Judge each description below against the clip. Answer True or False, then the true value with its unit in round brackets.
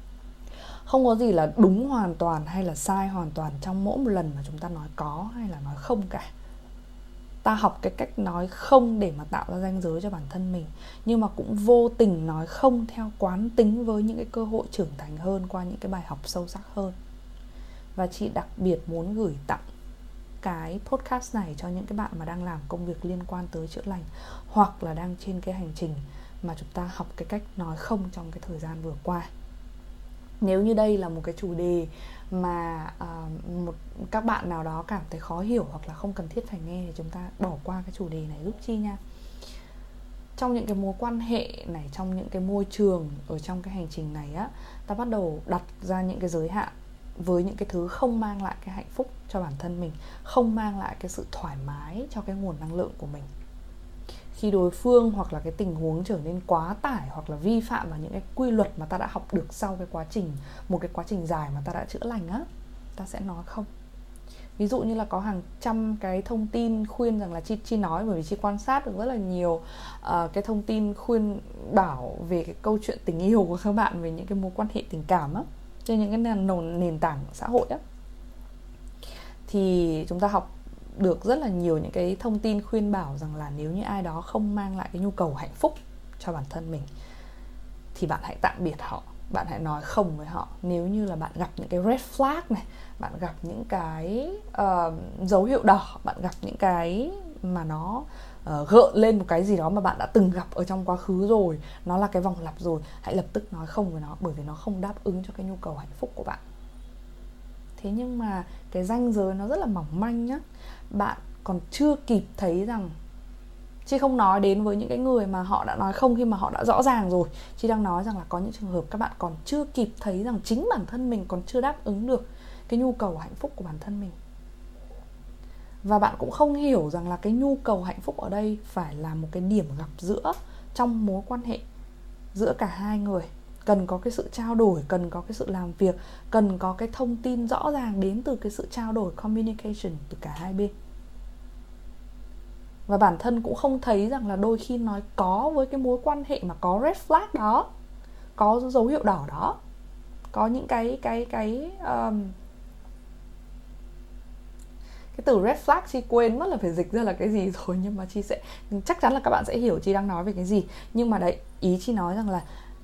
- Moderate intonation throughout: True (4.4 semitones)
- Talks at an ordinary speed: True (230 wpm)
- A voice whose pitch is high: True (195 Hz)